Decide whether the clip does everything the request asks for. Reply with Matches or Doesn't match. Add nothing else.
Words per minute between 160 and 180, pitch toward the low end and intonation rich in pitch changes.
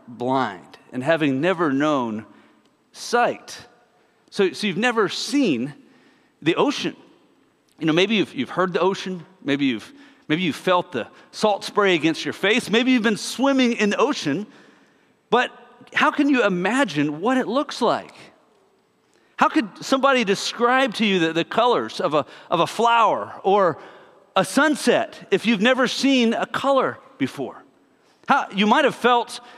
Doesn't match